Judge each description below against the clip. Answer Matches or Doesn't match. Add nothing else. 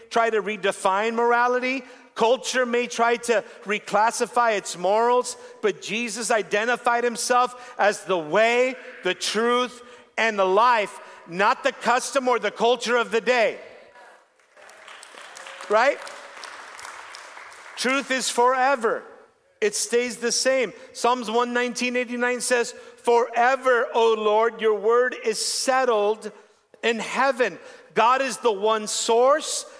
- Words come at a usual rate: Doesn't match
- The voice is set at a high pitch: Matches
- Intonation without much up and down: Matches